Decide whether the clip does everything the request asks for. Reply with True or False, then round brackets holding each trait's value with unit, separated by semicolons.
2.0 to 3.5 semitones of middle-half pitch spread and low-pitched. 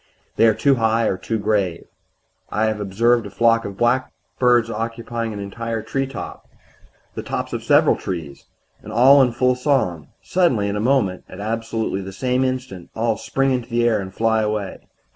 True (3.1 semitones; 115 Hz)